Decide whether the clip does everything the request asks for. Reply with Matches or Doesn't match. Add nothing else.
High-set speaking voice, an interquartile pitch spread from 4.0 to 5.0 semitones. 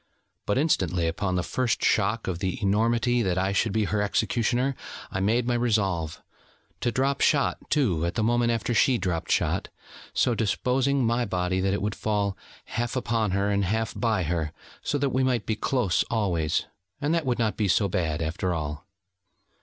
Doesn't match